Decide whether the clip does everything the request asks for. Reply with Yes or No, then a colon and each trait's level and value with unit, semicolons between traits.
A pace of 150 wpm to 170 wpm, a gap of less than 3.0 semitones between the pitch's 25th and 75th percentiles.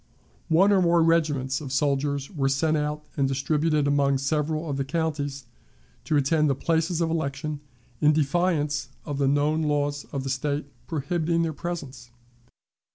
Yes: average, 160 wpm; narrow, 2.6 semitones